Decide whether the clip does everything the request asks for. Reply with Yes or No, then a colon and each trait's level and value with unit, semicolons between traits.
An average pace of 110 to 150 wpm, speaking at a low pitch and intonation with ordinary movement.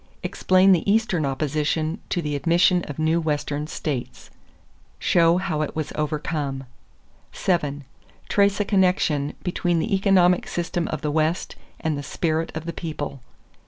No: average, 145 wpm; medium, 160 Hz; average, 3.1 semitones